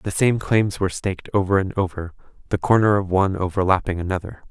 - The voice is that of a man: Yes, male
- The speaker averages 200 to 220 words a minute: No, average, 185 wpm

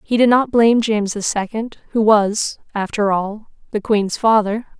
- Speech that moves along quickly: No, average, 175 wpm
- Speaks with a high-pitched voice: Yes, high, 215 Hz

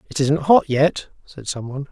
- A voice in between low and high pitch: Yes, medium, 145 Hz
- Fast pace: No, average, 190 wpm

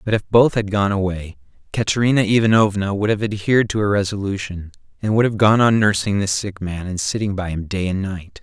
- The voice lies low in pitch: Yes, low, 100 Hz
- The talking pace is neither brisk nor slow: No, fast, 215 wpm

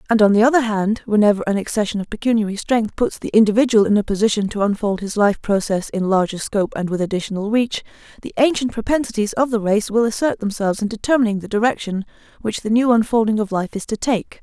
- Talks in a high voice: Yes, high, 215 Hz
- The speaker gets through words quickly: Yes, fast, 210 wpm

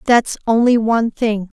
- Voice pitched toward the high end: Yes, high, 225 Hz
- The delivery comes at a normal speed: Yes, average, 150 wpm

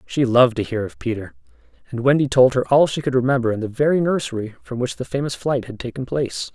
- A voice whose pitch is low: Yes, low, 125 Hz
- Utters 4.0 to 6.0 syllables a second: No, 6.4 syllables/s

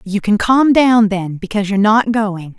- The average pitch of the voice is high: Yes, high, 210 Hz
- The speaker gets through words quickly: Yes, fast, 210 wpm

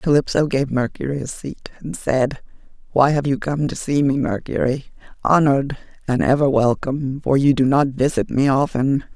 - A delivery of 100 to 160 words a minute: Yes, average, 155 wpm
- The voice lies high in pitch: No, medium, 140 Hz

